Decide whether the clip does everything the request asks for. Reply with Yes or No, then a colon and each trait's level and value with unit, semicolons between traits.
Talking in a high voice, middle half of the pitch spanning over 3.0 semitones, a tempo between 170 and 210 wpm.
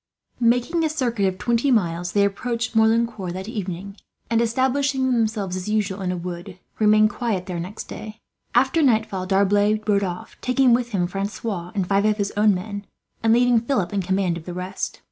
Yes: high, 210 Hz; average, 3.8 semitones; average, 185 wpm